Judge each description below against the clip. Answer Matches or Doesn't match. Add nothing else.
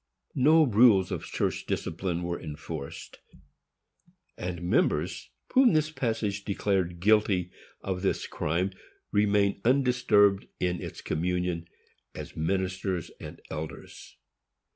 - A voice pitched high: Doesn't match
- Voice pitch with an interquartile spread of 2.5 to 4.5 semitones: Matches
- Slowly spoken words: Matches